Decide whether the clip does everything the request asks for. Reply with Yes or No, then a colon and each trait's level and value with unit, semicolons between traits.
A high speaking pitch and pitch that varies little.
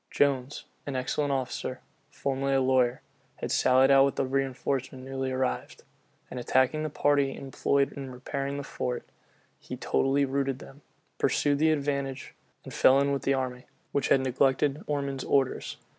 No: low, 135 Hz; narrow, 1.2 semitones